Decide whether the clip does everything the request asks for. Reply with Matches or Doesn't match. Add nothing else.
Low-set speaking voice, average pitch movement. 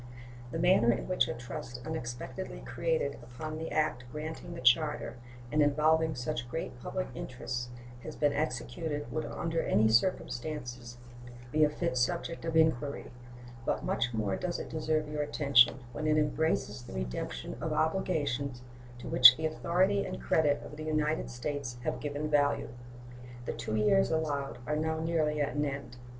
Doesn't match